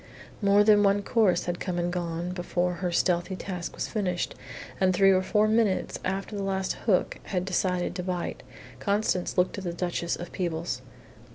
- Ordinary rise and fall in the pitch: No, narrow, 2.1 semitones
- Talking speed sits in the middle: Yes, average, 180 wpm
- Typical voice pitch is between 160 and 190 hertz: Yes, medium, 185 Hz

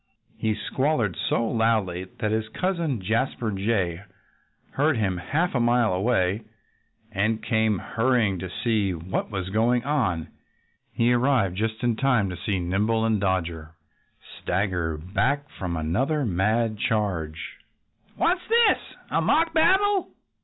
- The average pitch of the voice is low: Yes, low, 110 Hz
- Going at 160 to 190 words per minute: No, slow, 135 wpm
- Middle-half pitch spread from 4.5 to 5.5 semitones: Yes, average, 4.8 semitones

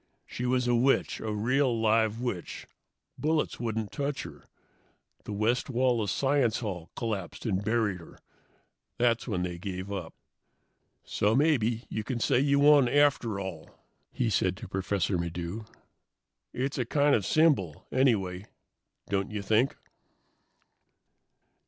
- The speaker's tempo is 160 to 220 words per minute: No, average, 140 wpm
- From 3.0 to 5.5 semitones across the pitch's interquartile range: Yes, average, 4.7 semitones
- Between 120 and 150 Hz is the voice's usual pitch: No, low, 110 Hz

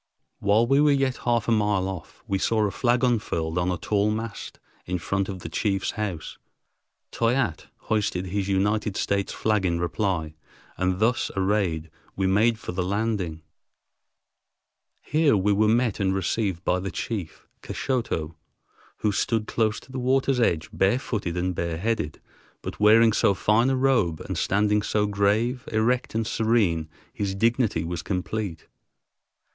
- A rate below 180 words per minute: Yes, average, 155 wpm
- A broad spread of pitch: No, average, 3.7 semitones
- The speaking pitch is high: No, low, 105 Hz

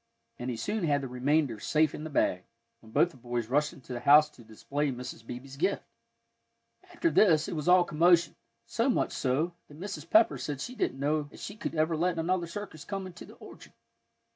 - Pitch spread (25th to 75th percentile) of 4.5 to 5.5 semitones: Yes, average, 5.0 semitones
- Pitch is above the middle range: No, medium, 150 Hz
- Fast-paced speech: Yes, fast, 210 wpm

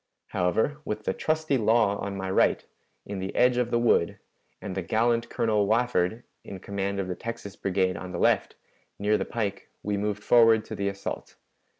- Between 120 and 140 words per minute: No, average, 190 wpm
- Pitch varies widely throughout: No, average, 3.1 semitones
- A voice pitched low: Yes, low, 105 Hz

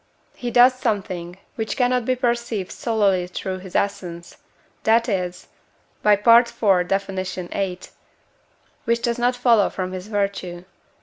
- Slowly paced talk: Yes, slow, 130 wpm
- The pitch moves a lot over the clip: No, average, 4.2 semitones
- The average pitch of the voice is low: No, high, 200 Hz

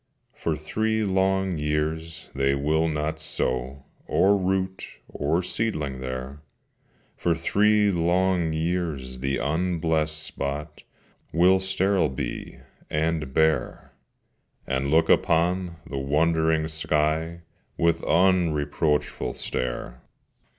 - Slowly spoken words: Yes, slow, 100 wpm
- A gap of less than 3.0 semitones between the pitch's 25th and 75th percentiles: No, average, 3.3 semitones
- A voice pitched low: Yes, very low, 80 Hz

